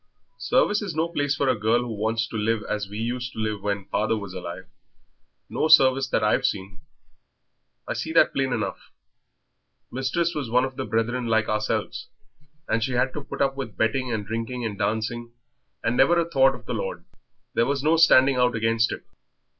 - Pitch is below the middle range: Yes, low, 120 Hz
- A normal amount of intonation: Yes, average, 3.4 semitones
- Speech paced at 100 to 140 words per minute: No, average, 195 wpm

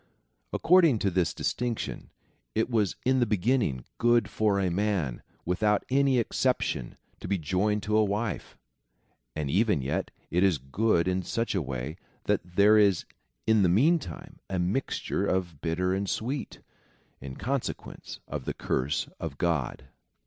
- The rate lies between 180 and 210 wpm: No, average, 155 wpm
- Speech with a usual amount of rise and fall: Yes, average, 4.9 semitones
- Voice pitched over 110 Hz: No, low, 100 Hz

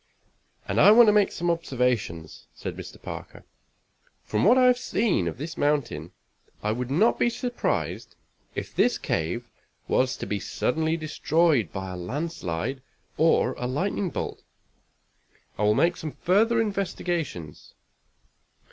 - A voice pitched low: No, medium, 150 Hz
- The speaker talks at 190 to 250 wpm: No, average, 140 wpm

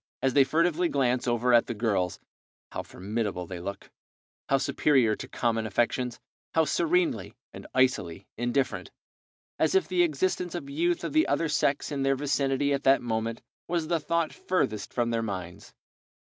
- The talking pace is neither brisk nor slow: Yes, average, 165 wpm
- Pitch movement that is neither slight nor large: No, wide, 5.8 semitones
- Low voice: Yes, low, 130 Hz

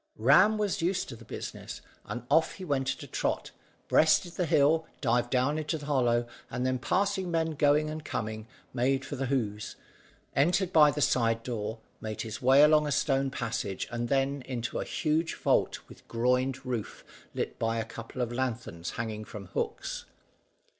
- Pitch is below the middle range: Yes, low, 130 Hz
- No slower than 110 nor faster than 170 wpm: No, average, 180 wpm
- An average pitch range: Yes, average, 4.4 semitones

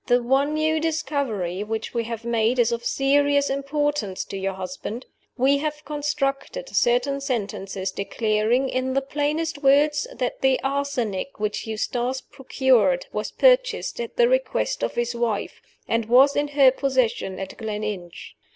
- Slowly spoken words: No, average, 150 wpm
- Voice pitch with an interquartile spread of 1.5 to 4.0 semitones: No, average, 4.5 semitones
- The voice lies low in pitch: No, very high, 260 Hz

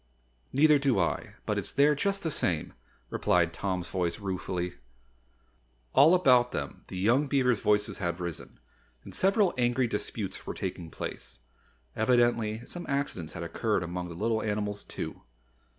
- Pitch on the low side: Yes, low, 110 Hz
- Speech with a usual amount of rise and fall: No, wide, 7.1 semitones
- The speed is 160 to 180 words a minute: No, average, 150 wpm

